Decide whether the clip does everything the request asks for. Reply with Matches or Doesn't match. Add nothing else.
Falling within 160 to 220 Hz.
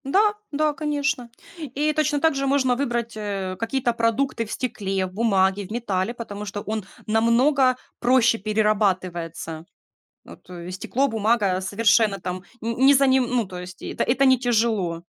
Doesn't match